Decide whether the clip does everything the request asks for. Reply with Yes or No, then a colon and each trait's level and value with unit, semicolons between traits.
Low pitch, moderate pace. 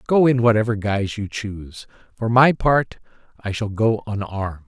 Yes: low, 110 Hz; average, 165 wpm